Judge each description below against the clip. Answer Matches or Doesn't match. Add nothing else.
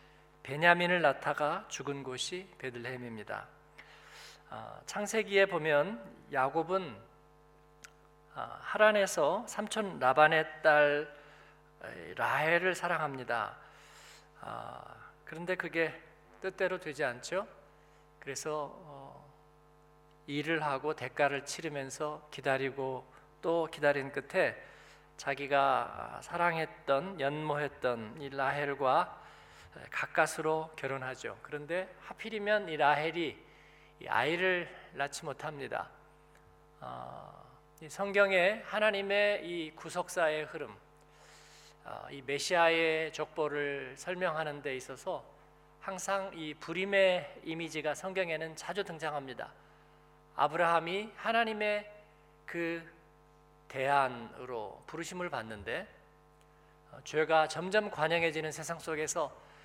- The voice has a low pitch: Doesn't match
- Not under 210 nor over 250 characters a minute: Matches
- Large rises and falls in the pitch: Doesn't match